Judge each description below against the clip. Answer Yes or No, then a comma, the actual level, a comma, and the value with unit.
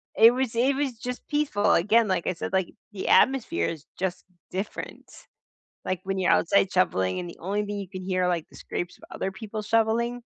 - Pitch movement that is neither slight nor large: Yes, average, 4.0 semitones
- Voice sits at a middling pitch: No, high, 200 Hz